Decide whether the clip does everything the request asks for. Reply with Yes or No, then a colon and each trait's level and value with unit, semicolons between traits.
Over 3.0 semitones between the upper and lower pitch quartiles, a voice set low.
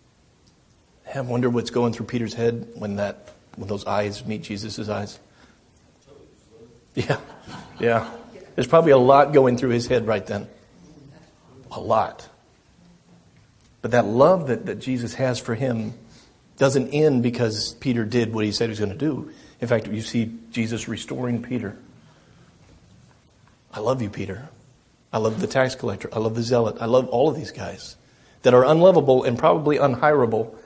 No: average, 2.7 semitones; low, 120 Hz